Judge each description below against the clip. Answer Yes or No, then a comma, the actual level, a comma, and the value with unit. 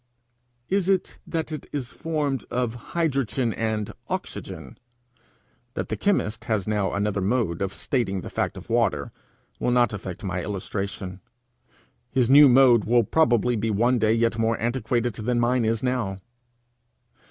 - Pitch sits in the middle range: No, low, 115 Hz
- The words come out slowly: No, average, 150 wpm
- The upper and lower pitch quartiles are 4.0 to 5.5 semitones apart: No, average, 3.4 semitones